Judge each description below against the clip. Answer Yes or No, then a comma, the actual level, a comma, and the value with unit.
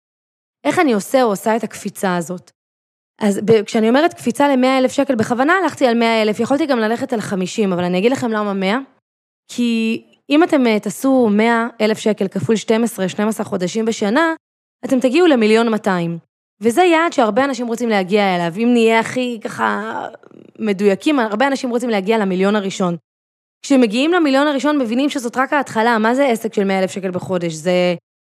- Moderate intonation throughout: Yes, average, 4.5 semitones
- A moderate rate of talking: No, fast, 165 wpm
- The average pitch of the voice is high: Yes, high, 225 Hz